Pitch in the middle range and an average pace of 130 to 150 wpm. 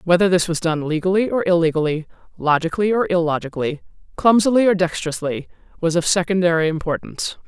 Yes: medium, 175 Hz; slow, 135 wpm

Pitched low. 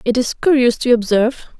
No: high, 245 Hz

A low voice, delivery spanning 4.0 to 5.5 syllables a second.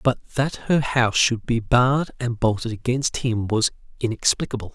Yes: low, 120 Hz; 4.9 syllables/s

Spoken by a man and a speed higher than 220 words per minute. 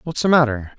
Yes: male; fast, 230 wpm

